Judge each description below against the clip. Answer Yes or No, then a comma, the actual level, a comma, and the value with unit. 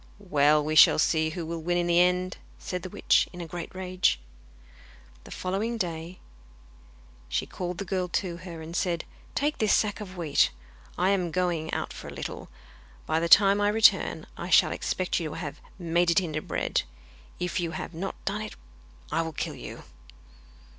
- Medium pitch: Yes, medium, 175 Hz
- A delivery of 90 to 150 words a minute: No, average, 190 wpm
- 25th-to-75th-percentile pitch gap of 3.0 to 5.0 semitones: No, narrow, 2.4 semitones